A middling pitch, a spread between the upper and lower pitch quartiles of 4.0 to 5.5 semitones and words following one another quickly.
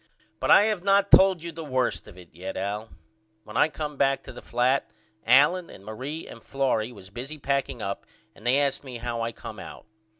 No: low, 130 Hz; average, 5.1 semitones; fast, 210 wpm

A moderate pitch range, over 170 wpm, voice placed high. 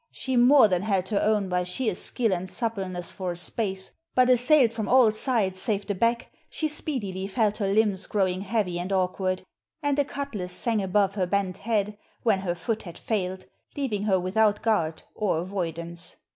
Yes: average, 3.6 semitones; average, 185 wpm; high, 200 Hz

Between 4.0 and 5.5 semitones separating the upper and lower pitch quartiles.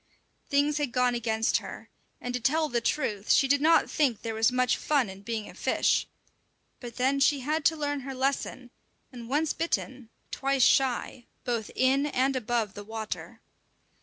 No: average, 3.3 semitones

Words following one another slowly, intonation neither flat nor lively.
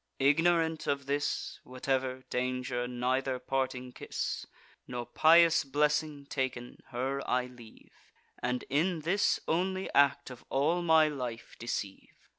Yes: slow, 120 wpm; average, 3.7 semitones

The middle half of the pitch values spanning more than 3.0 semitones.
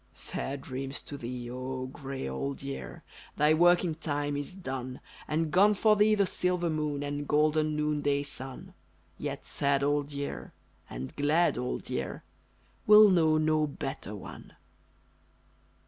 No: average, 2.7 semitones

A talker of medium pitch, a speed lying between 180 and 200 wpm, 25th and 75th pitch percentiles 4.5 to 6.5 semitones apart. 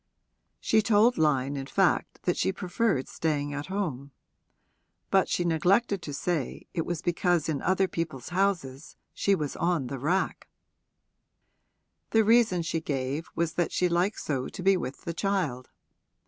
No: medium, 170 Hz; average, 155 wpm; average, 4.9 semitones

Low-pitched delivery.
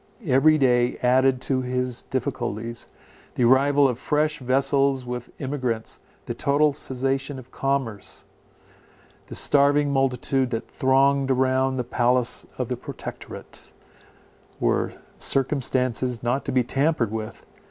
Yes: low, 130 Hz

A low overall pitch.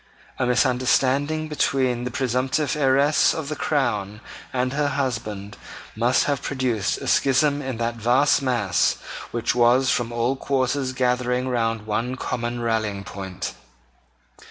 Yes: low, 125 Hz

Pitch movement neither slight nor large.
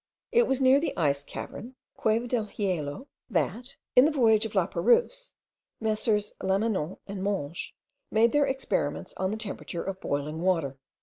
No: wide, 5.8 semitones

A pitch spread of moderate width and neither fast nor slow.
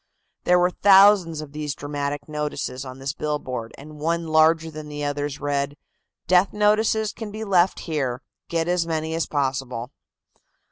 Yes: average, 3.7 semitones; average, 155 wpm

